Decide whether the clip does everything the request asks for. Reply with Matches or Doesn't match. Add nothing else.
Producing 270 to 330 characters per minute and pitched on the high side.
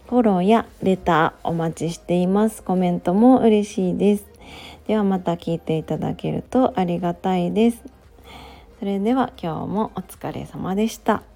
Matches